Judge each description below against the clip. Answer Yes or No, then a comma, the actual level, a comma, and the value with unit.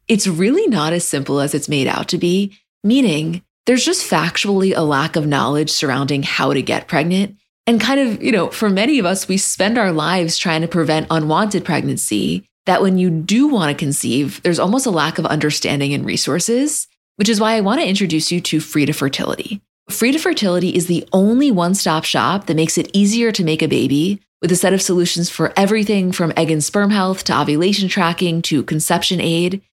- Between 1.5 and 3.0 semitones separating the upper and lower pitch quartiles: No, average, 4.2 semitones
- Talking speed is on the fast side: Yes, fast, 210 wpm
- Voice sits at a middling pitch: Yes, medium, 180 Hz